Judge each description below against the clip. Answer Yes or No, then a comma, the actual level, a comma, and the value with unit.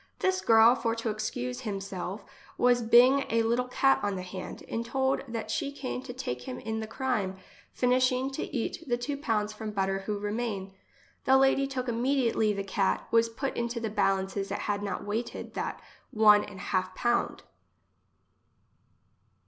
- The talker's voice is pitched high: Yes, high, 230 Hz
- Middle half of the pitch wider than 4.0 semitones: No, average, 3.5 semitones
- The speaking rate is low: No, average, 175 wpm